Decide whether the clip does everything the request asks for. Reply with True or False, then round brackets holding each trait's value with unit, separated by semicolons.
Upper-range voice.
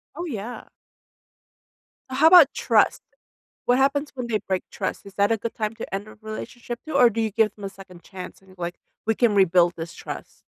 True (215 Hz)